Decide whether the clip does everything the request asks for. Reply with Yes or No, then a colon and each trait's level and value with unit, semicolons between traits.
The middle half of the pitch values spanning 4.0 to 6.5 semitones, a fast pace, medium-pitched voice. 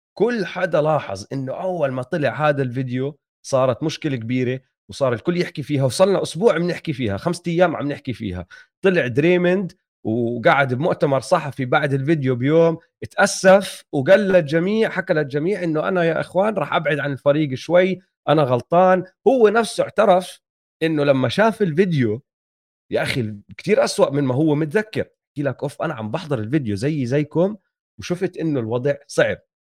Yes: average, 5.1 semitones; fast, 155 wpm; medium, 155 Hz